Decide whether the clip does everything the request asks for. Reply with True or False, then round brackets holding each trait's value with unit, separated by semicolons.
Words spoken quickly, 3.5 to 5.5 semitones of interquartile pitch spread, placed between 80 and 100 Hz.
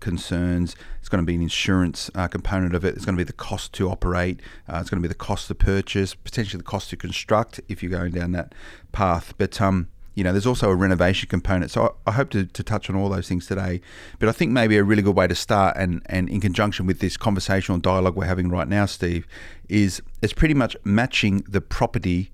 False (240 wpm; 2.4 semitones; 95 Hz)